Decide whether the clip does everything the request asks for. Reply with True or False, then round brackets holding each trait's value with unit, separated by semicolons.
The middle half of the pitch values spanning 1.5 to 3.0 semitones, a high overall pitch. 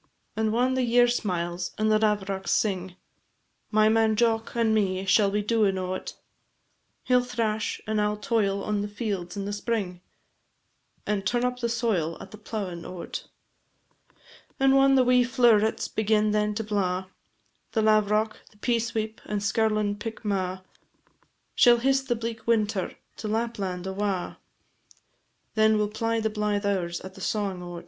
True (2.5 semitones; 215 Hz)